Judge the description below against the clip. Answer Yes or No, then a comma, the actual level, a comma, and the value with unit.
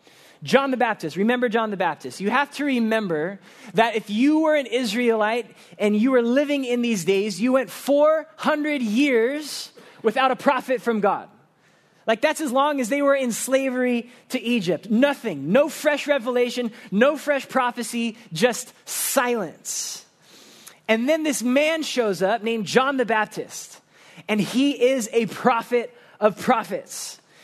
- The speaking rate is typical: Yes, average, 155 wpm